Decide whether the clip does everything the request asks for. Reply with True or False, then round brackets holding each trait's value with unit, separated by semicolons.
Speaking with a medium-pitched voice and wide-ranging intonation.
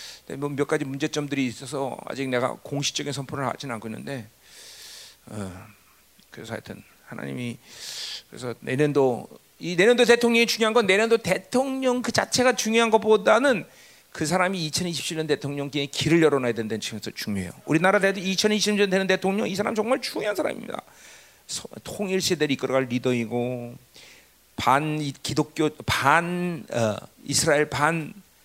True (150 Hz; 6.7 semitones)